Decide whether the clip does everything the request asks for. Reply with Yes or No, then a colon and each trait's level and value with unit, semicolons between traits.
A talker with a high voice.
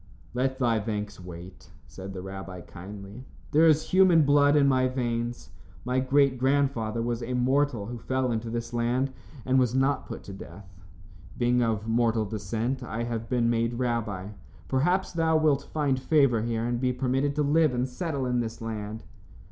No: low, 120 Hz